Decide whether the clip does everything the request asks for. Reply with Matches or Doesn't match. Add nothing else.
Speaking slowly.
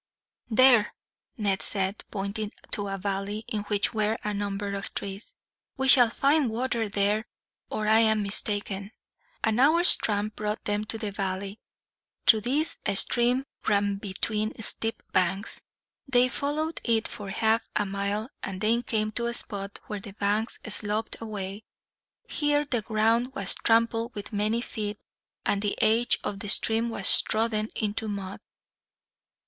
Doesn't match